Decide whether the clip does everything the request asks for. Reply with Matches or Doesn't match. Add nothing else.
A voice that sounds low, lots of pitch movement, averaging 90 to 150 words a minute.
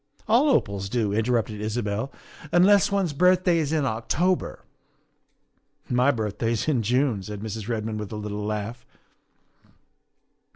Matches